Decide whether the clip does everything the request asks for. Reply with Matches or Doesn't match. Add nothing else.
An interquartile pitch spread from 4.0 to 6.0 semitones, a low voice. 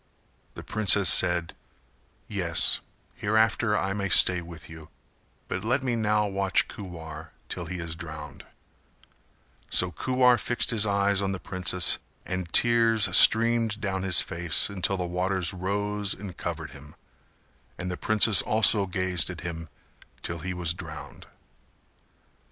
Doesn't match